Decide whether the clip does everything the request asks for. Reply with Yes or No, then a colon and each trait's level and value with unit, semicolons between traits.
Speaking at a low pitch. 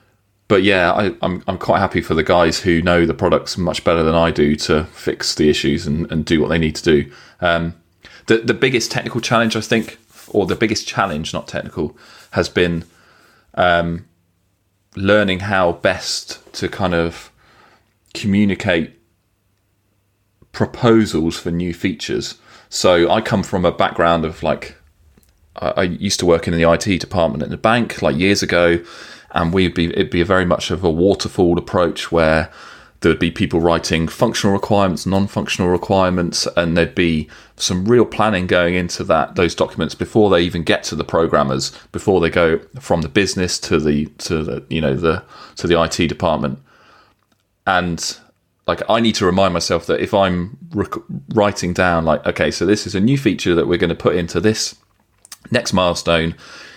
Yes: very low, 90 Hz